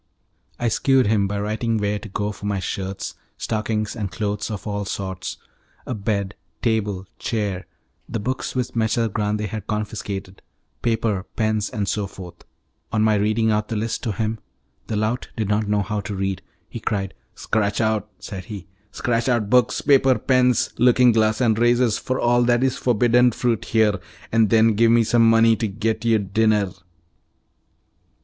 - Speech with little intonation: Yes, narrow, 2.1 semitones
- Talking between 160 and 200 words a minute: Yes, average, 170 wpm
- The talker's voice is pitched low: Yes, low, 110 Hz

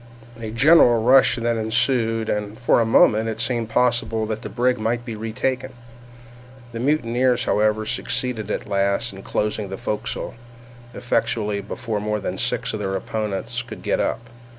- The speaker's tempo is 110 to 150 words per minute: No, average, 160 wpm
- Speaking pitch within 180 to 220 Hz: No, low, 115 Hz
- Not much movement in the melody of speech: Yes, narrow, 2.2 semitones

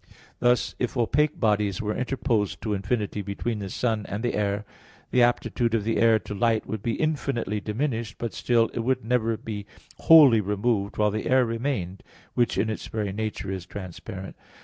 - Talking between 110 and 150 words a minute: No, average, 180 wpm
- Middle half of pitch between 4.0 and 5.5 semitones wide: No, average, 2.7 semitones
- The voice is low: Yes, low, 110 Hz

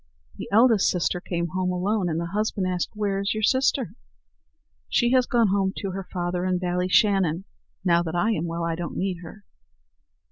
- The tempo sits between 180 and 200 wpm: Yes, average, 185 wpm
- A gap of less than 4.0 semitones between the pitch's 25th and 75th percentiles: Yes, average, 3.0 semitones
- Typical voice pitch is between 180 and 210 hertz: Yes, medium, 185 Hz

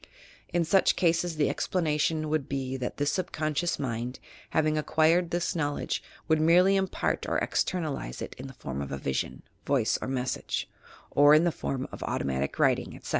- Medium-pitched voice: Yes, medium, 155 Hz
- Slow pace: No, average, 175 wpm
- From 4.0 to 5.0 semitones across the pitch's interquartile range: Yes, average, 4.3 semitones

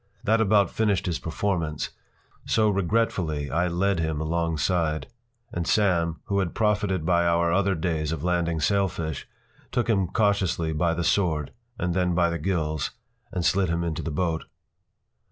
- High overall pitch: No, very low, 85 Hz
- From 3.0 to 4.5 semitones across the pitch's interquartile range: Yes, average, 3.3 semitones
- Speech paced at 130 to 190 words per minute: Yes, average, 155 wpm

